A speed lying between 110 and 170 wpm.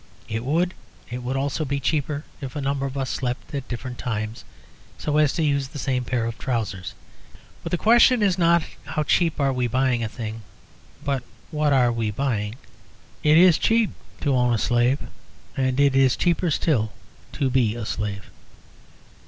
No: average, 185 wpm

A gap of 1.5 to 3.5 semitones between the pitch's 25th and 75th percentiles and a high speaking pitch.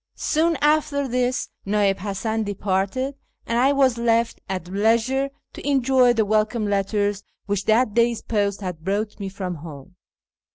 No: average, 4.2 semitones; high, 215 Hz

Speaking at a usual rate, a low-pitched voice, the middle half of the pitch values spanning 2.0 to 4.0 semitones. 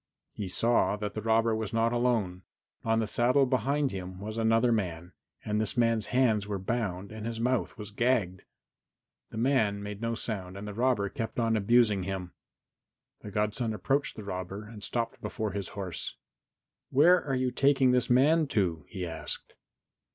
Yes: average, 175 wpm; low, 110 Hz; average, 3.4 semitones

